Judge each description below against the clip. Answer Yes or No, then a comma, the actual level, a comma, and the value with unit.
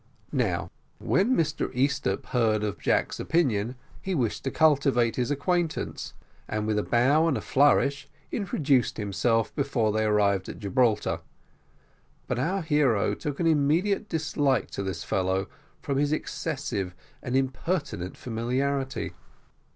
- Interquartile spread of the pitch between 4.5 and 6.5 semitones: Yes, wide, 5.6 semitones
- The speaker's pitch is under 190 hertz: Yes, low, 135 Hz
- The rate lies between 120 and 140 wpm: Yes, slow, 135 wpm